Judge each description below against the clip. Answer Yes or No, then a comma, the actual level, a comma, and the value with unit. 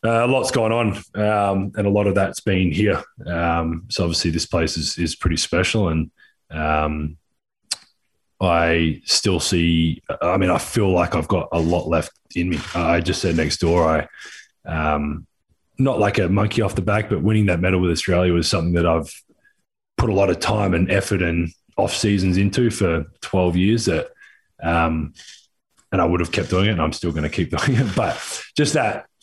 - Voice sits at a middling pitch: No, very low, 90 Hz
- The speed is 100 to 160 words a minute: No, average, 200 wpm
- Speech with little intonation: No, average, 3.6 semitones